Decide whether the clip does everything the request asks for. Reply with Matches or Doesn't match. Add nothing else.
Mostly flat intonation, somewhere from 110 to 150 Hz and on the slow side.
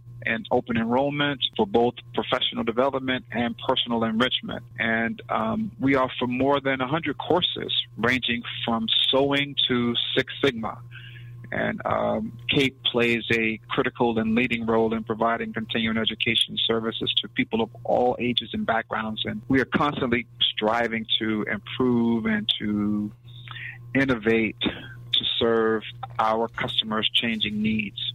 Matches